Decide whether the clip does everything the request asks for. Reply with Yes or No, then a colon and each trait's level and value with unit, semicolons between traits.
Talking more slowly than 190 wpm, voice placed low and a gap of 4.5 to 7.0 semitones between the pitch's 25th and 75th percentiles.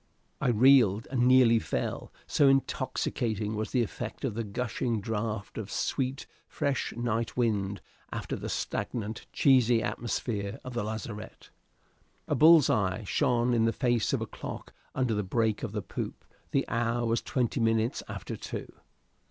No: average, 155 wpm; low, 115 Hz; narrow, 2.5 semitones